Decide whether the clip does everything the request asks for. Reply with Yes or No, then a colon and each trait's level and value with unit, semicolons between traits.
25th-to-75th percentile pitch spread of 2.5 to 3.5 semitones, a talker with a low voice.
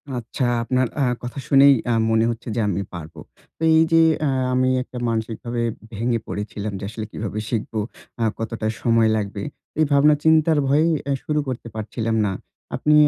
No: average, 4.1 semitones; low, 115 Hz